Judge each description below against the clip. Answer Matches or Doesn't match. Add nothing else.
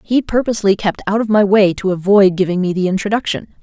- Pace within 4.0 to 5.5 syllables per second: Doesn't match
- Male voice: Doesn't match